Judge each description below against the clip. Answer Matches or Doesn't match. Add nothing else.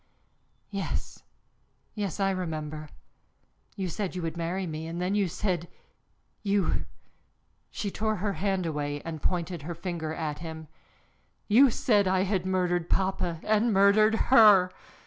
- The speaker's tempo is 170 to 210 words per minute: Doesn't match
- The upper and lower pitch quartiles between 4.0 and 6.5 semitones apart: Doesn't match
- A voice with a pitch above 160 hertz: Matches